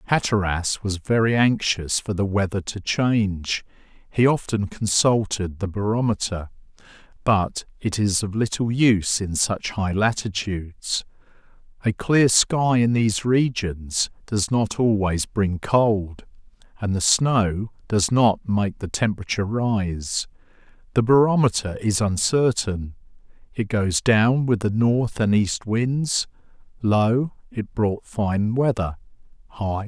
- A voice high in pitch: No, low, 105 Hz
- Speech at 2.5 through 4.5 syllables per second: Yes, 4.0 syllables/s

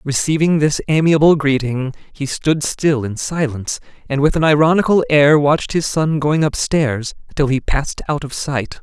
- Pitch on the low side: No, medium, 145 Hz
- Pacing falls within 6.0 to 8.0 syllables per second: No, 4.8 syllables/s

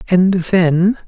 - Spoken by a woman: No, male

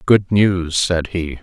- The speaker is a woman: No, male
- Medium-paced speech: Yes, average, 170 wpm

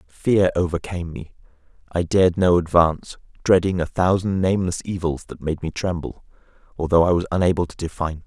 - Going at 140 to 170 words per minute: Yes, average, 165 wpm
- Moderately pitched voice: No, very low, 85 Hz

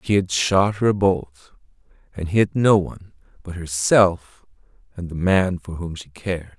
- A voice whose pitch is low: Yes, very low, 90 Hz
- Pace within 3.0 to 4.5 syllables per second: Yes, 4.1 syllables/s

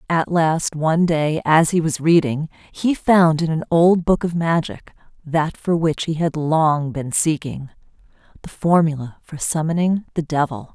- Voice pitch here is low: No, medium, 160 Hz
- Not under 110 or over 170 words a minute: Yes, average, 160 wpm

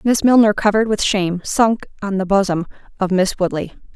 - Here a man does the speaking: No, female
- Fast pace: No, average, 180 wpm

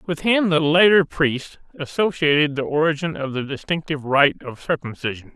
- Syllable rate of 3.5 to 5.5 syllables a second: Yes, 5.1 syllables/s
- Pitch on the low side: No, medium, 150 Hz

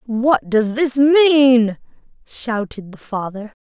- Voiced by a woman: Yes, female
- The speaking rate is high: No, slow, 115 wpm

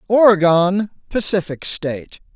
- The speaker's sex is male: Yes, male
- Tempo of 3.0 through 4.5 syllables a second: Yes, 4.3 syllables/s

